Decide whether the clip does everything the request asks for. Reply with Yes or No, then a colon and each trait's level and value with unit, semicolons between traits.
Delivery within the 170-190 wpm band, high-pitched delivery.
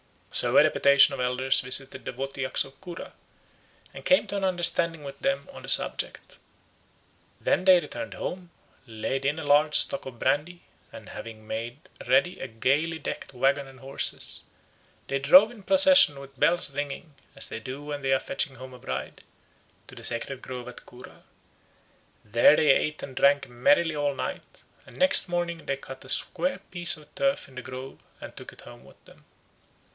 No: average, 180 wpm; medium, 140 Hz